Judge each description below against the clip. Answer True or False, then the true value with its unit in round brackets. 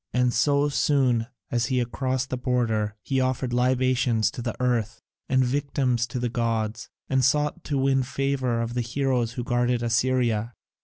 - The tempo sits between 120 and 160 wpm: False (175 wpm)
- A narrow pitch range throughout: True (2.0 semitones)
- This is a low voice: True (125 Hz)